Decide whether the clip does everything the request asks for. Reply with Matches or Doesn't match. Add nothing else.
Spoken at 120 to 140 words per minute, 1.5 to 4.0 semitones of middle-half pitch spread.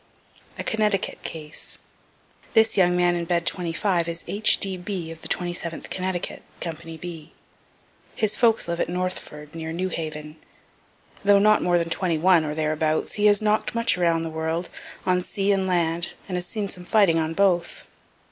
Doesn't match